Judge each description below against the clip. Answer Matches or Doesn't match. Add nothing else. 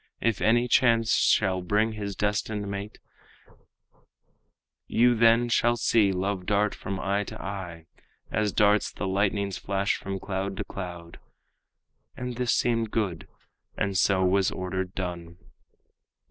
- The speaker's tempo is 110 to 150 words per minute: Matches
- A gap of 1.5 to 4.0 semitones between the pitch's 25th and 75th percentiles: Matches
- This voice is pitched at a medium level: Doesn't match